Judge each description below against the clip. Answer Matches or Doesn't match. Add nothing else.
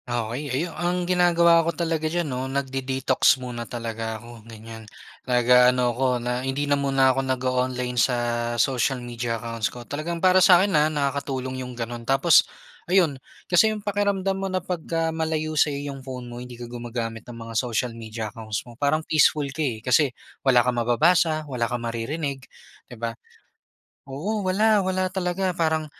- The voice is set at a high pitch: Doesn't match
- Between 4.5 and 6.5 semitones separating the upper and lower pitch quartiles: Matches